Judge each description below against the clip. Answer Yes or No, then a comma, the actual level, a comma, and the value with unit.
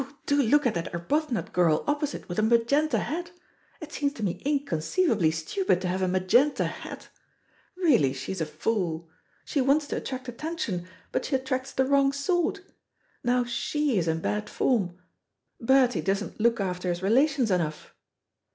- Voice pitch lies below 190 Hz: No, high, 235 Hz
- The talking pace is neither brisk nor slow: Yes, average, 165 wpm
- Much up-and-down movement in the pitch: Yes, wide, 7.9 semitones